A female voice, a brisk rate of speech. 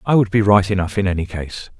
No: male; fast, 270 wpm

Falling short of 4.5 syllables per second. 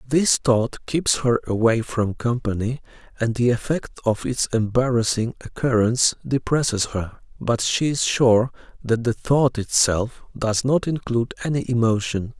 Yes: 4.3 syllables/s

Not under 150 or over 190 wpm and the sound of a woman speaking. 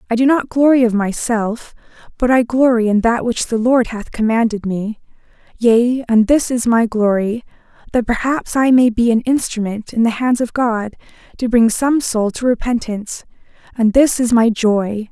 Yes: average, 185 wpm; female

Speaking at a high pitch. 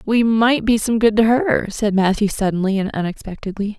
Yes: high, 215 Hz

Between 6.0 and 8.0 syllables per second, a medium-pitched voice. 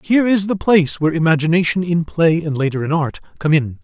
Yes: 6.2 syllables/s; medium, 165 Hz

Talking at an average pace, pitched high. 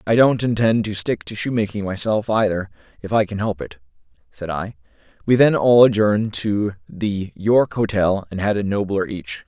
No: average, 185 wpm; low, 100 Hz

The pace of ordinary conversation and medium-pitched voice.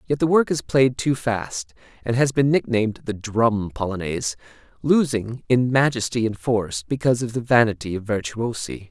No: average, 170 wpm; low, 115 Hz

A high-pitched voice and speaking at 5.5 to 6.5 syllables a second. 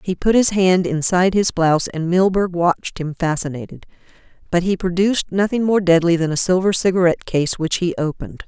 No: medium, 175 Hz; 5.7 syllables/s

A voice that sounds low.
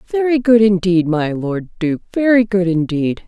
No: high, 195 Hz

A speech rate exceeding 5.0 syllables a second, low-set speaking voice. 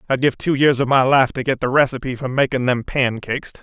Yes: 6.0 syllables/s; low, 130 Hz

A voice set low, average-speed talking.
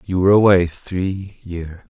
Yes: very low, 90 Hz; average, 155 wpm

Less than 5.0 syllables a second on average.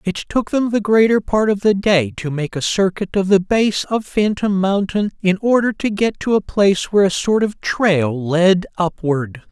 Yes: 4.5 syllables/s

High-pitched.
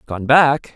No: low, 130 Hz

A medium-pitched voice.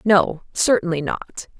Yes: medium, 180 Hz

